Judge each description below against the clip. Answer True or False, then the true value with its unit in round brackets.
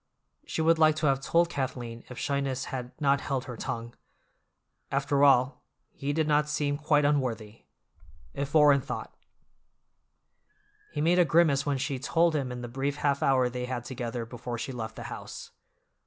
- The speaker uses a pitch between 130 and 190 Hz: True (140 Hz)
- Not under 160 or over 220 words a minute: True (170 wpm)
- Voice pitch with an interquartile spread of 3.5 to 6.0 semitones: False (3.0 semitones)